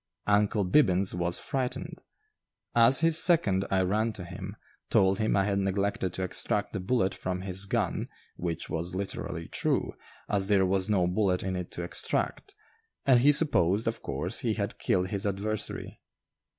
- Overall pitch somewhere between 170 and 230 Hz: No, low, 100 Hz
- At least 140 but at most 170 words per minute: Yes, average, 165 wpm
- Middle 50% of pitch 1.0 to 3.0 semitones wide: Yes, average, 2.7 semitones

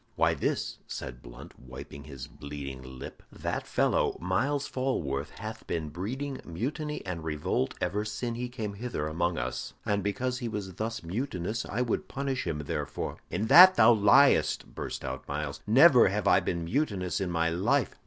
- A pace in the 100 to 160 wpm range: No, average, 170 wpm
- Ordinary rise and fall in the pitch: No, wide, 7.6 semitones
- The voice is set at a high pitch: No, low, 100 Hz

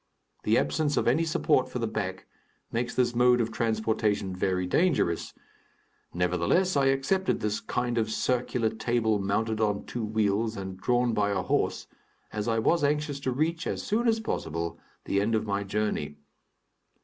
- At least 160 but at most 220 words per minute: Yes, average, 165 wpm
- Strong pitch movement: No, average, 4.4 semitones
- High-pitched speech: No, low, 110 Hz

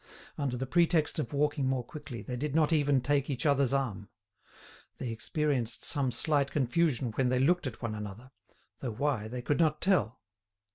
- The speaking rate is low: No, average, 180 wpm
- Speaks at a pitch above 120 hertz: Yes, low, 135 Hz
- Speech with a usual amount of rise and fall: Yes, average, 3.4 semitones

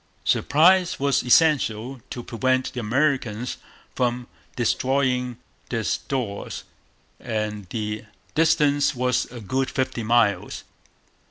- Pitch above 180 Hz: No, low, 125 Hz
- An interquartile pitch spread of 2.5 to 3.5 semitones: Yes, average, 3.2 semitones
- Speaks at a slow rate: Yes, slow, 100 wpm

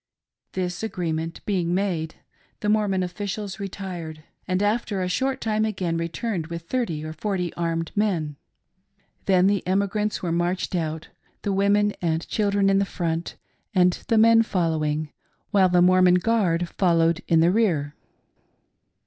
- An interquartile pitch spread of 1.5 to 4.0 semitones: Yes, average, 3.4 semitones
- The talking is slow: No, average, 150 wpm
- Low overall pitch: No, medium, 185 Hz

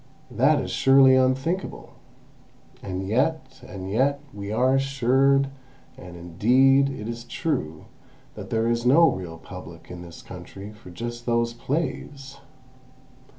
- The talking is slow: Yes, slow, 120 wpm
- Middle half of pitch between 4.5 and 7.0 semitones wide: Yes, average, 5.0 semitones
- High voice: No, low, 120 Hz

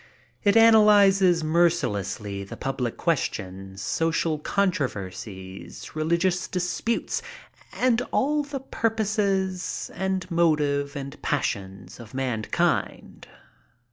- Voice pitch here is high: No, medium, 170 Hz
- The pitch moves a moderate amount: No, wide, 8.7 semitones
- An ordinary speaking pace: No, slow, 95 wpm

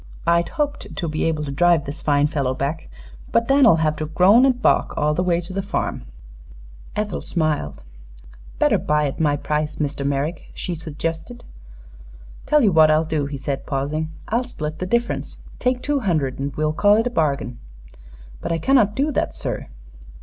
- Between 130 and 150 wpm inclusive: No, average, 185 wpm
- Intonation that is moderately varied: No, wide, 5.8 semitones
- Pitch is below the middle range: No, medium, 160 Hz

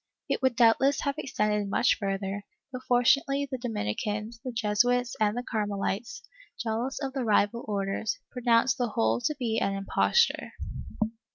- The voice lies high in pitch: Yes, high, 230 Hz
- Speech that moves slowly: No, average, 150 wpm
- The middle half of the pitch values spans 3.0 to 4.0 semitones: Yes, average, 3.5 semitones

